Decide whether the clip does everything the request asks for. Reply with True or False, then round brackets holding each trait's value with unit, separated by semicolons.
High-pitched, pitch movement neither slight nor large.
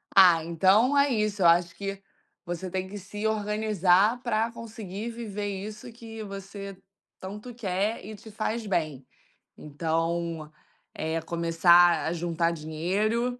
True (195 Hz; 4.2 semitones)